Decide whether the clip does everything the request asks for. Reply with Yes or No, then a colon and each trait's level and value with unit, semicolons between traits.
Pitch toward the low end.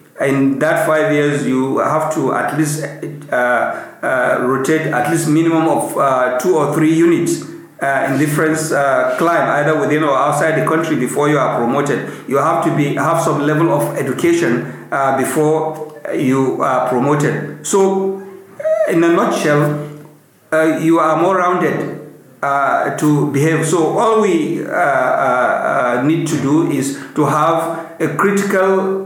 No: medium, 155 Hz